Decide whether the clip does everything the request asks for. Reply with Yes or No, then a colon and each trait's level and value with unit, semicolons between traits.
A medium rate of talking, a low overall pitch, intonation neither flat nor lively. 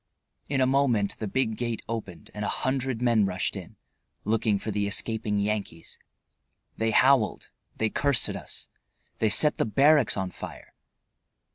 Yes: average, 155 wpm; low, 110 Hz; average, 4.1 semitones